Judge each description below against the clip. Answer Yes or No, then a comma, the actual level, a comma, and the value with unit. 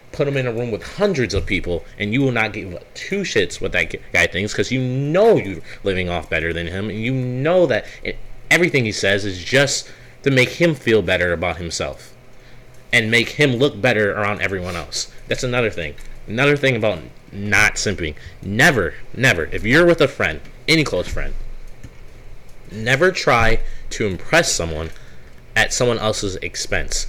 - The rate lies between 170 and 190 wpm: Yes, average, 180 wpm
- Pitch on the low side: Yes, low, 115 Hz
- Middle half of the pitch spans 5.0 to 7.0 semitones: Yes, wide, 5.6 semitones